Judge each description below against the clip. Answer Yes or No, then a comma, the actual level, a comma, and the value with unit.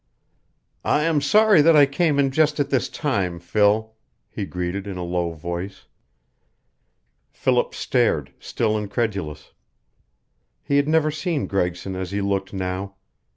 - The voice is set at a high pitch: No, low, 105 Hz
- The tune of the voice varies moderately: No, wide, 7.6 semitones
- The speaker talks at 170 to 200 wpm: No, average, 140 wpm